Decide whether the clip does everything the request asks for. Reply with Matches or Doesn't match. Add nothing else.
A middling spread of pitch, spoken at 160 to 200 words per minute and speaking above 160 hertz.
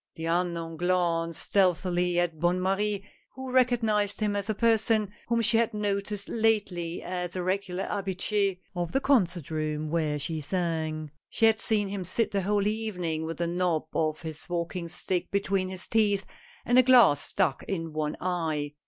Matches